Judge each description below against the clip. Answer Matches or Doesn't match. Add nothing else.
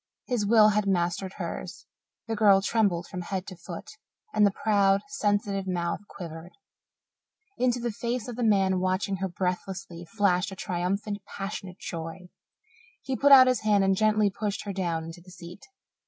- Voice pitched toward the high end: Matches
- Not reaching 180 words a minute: Matches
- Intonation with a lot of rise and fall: Doesn't match